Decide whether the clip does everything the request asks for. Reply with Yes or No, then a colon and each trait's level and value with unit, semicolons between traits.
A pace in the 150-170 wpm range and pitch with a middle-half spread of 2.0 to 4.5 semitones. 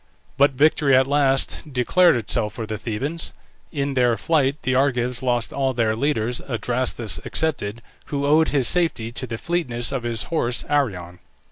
Yes: average, 160 wpm; average, 3.5 semitones